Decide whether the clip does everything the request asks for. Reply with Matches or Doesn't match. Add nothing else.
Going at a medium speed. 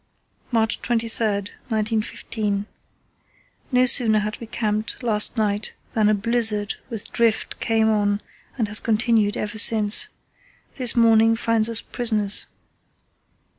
Doesn't match